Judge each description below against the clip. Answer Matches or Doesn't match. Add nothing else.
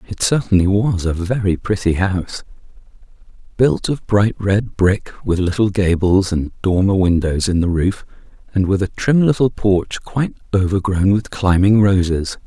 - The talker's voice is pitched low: Matches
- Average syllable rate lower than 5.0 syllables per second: Matches